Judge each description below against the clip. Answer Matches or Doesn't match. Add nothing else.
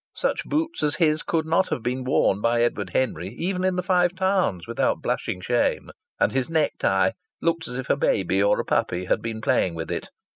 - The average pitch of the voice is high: Doesn't match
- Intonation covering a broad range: Matches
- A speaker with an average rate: Doesn't match